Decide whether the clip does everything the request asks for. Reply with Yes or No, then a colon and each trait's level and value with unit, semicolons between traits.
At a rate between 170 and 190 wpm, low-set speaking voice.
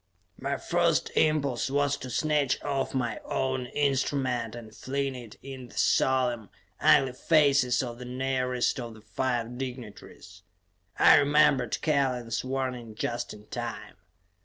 No: slow, 135 wpm; low, 130 Hz